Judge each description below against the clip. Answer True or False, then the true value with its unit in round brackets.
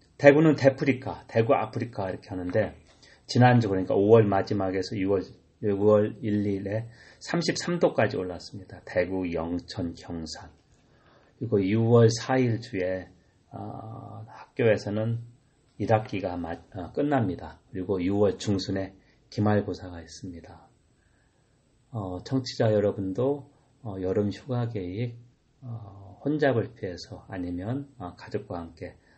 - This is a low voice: True (105 Hz)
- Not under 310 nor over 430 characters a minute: False (230 characters per minute)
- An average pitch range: True (4.9 semitones)